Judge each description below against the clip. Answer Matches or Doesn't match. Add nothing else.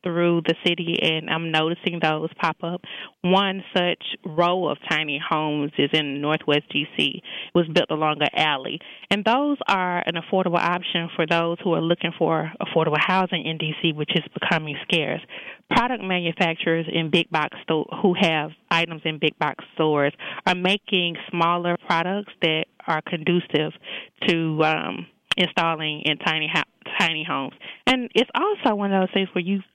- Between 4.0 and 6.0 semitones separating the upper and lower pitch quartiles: Doesn't match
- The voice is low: Doesn't match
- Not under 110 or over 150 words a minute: Doesn't match